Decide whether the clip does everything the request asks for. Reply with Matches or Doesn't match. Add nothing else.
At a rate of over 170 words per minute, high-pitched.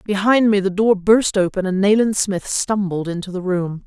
Matches